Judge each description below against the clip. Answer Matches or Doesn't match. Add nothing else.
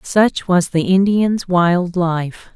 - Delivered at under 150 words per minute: Matches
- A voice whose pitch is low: Doesn't match